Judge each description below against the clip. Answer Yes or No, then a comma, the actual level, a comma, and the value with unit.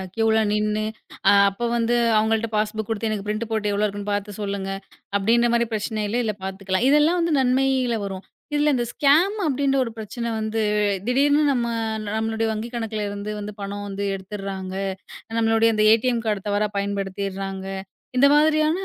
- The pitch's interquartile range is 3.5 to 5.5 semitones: No, average, 2.9 semitones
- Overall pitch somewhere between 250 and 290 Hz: No, high, 220 Hz